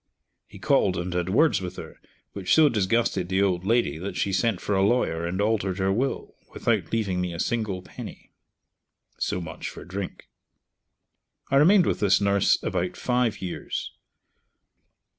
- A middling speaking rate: Yes, average, 160 wpm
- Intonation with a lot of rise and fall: No, average, 3.9 semitones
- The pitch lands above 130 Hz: No, low, 100 Hz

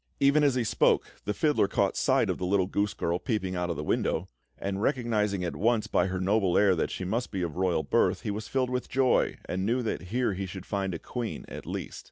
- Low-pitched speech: Yes, low, 100 Hz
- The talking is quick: Yes, fast, 245 wpm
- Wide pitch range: No, average, 4.3 semitones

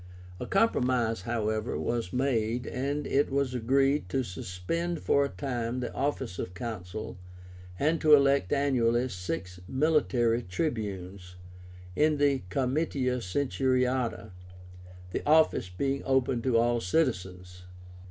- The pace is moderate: No, slow, 120 wpm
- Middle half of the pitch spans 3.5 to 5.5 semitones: Yes, average, 4.4 semitones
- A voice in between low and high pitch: No, low, 125 Hz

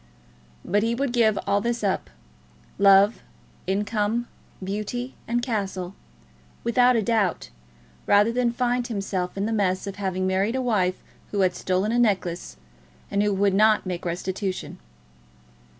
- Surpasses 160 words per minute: No, average, 145 wpm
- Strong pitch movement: No, average, 3.5 semitones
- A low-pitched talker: No, high, 205 Hz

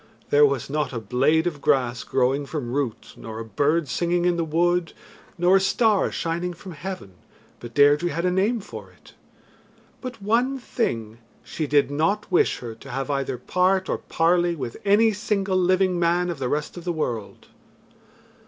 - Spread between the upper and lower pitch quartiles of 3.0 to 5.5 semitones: Yes, average, 5.1 semitones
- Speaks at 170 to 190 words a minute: Yes, average, 180 wpm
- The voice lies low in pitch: No, medium, 165 Hz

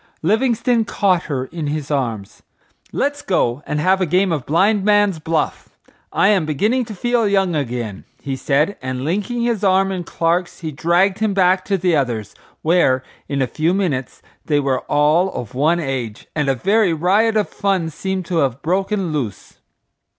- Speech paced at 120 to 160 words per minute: No, average, 180 wpm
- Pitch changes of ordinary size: No, wide, 5.7 semitones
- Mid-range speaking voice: Yes, medium, 170 Hz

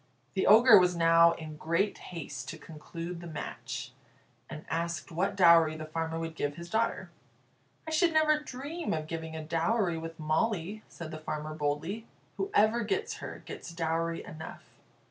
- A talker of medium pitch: Yes, medium, 165 Hz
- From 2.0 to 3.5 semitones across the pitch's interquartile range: No, average, 4.3 semitones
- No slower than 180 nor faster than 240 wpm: No, average, 165 wpm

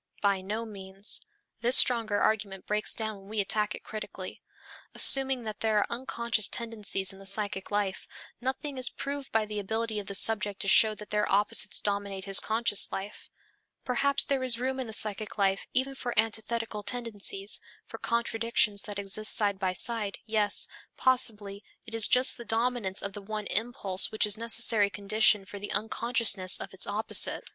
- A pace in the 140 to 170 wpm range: No, average, 180 wpm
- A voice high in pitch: Yes, high, 215 Hz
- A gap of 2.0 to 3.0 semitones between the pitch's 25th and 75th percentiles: Yes, narrow, 2.5 semitones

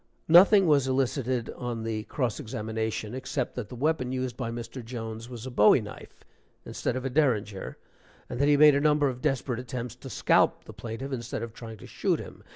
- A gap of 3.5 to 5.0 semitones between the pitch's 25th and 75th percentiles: No, average, 3.0 semitones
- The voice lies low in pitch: Yes, low, 125 Hz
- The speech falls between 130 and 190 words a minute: No, average, 200 wpm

